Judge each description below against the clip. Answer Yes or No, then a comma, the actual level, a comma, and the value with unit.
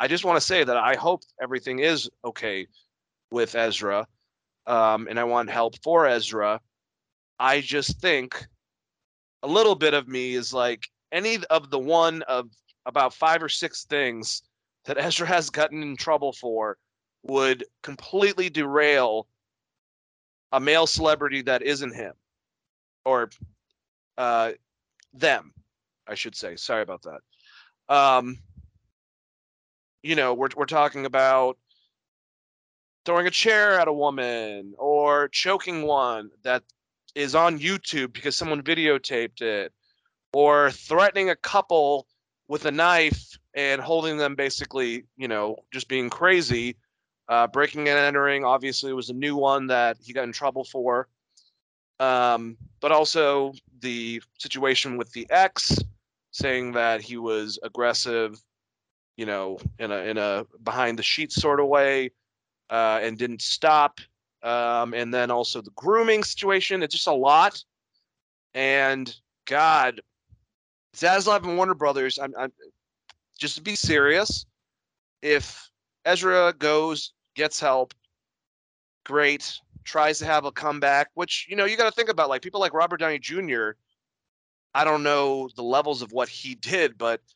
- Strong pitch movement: No, average, 4.4 semitones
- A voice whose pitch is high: No, low, 135 Hz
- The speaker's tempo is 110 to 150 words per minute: Yes, average, 140 wpm